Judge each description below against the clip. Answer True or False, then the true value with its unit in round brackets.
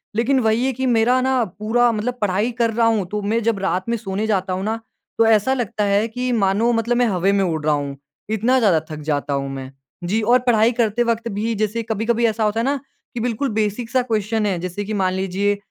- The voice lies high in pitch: True (220 Hz)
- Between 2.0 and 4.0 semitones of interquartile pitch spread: True (3.0 semitones)